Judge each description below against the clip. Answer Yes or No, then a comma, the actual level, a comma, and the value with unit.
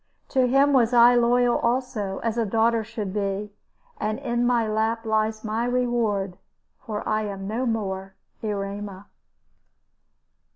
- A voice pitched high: Yes, high, 220 Hz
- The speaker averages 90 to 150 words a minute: Yes, slow, 135 wpm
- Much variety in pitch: No, narrow, 2.6 semitones